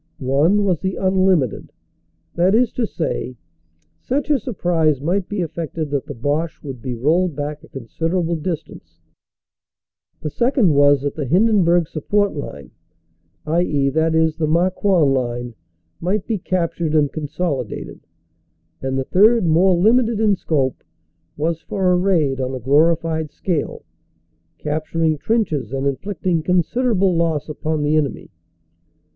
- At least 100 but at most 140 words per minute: Yes, slow, 135 wpm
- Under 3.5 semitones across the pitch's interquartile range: No, average, 4.4 semitones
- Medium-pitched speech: Yes, medium, 160 Hz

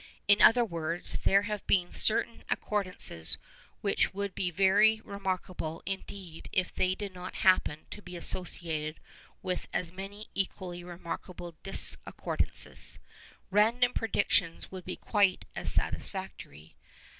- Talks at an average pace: No, slow, 120 wpm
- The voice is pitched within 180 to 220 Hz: Yes, medium, 185 Hz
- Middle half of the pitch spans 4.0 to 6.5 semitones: No, narrow, 2.5 semitones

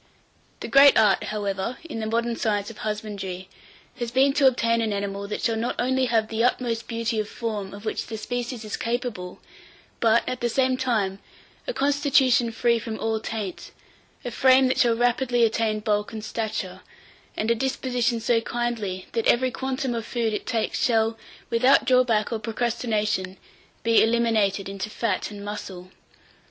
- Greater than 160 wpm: Yes, average, 170 wpm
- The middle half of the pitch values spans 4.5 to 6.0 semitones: No, narrow, 2.5 semitones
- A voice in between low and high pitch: No, high, 230 Hz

